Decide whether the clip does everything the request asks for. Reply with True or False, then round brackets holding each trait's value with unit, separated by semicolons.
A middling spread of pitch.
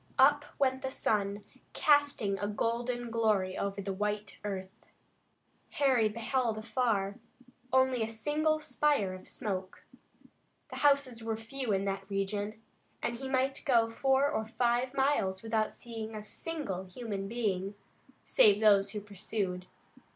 True (4.6 semitones)